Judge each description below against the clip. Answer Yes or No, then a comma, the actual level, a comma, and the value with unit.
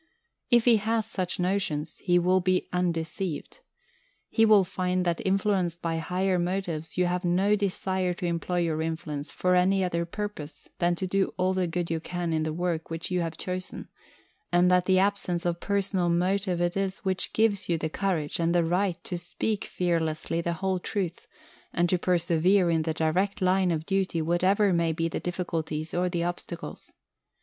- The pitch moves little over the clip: Yes, narrow, 2.1 semitones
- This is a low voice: No, medium, 180 Hz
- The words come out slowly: No, average, 185 wpm